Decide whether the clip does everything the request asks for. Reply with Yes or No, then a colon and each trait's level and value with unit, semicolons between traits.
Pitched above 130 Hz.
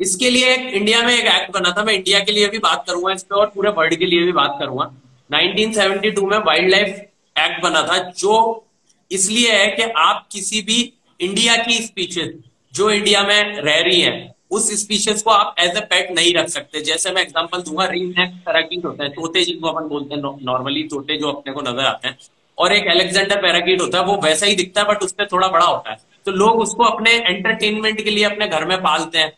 Yes: high, 190 Hz